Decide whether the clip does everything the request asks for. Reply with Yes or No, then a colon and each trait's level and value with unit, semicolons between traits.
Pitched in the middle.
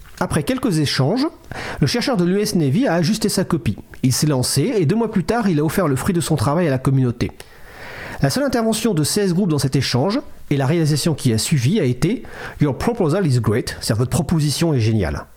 Yes: medium, 155 Hz